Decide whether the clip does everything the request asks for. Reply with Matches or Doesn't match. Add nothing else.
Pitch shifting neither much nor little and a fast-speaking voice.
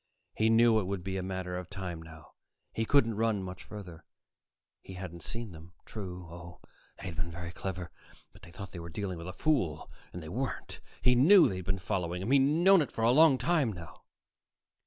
Matches